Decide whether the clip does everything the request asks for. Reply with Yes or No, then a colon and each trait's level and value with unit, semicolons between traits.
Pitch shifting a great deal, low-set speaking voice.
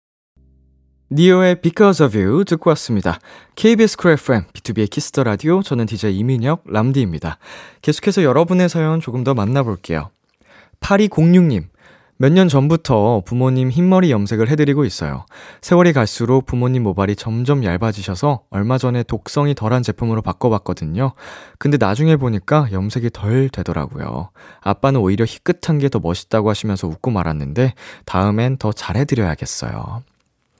Yes: wide, 6.4 semitones; low, 125 Hz